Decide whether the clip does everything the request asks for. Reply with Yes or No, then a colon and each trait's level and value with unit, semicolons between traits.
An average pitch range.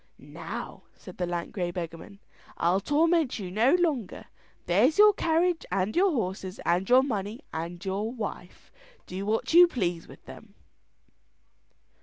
No: wide, 8.3 semitones